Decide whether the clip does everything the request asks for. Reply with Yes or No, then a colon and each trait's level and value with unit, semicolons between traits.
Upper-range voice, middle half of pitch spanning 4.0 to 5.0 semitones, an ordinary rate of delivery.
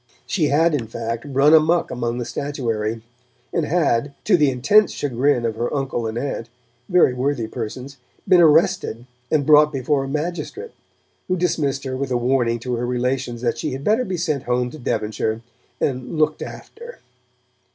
No: low, 135 Hz; average, 4.3 semitones; average, 170 wpm